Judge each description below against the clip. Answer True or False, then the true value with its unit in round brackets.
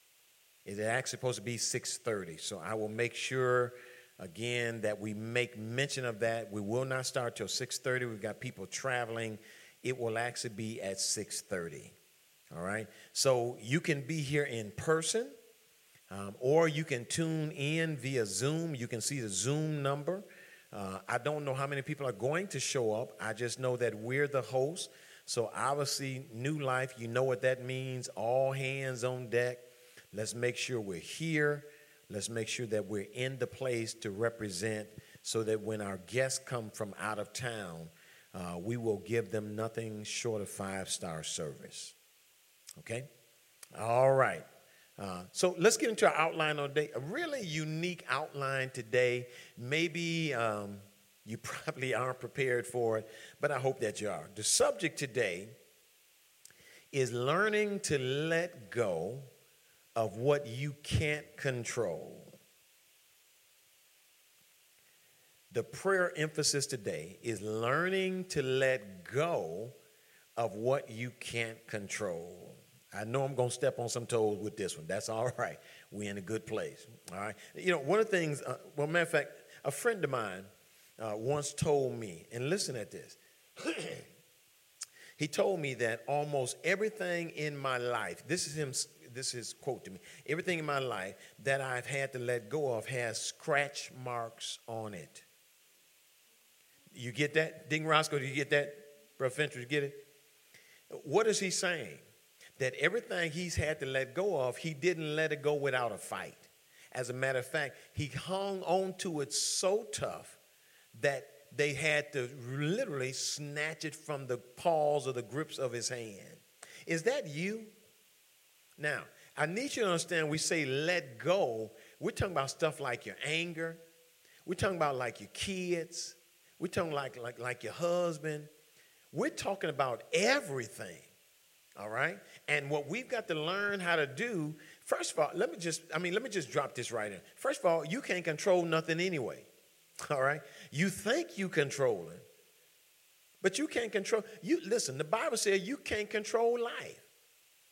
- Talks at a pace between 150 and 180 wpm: True (165 wpm)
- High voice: False (135 Hz)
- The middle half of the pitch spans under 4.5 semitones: False (5.3 semitones)